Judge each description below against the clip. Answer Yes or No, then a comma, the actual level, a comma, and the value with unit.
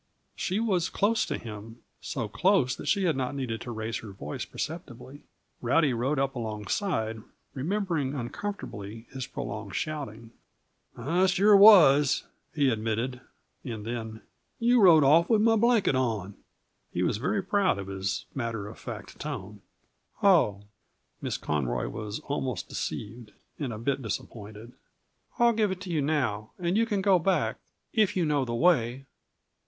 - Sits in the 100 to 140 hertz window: Yes, low, 135 Hz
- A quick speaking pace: No, average, 155 wpm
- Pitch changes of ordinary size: No, wide, 8.4 semitones